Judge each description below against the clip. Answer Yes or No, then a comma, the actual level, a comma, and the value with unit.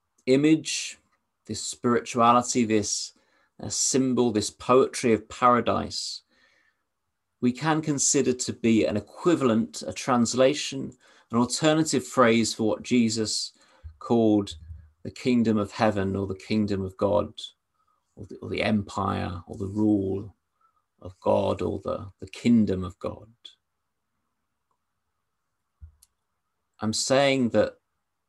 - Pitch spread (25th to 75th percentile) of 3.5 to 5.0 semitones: Yes, average, 4.0 semitones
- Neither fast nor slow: No, slow, 115 wpm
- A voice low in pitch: Yes, low, 110 Hz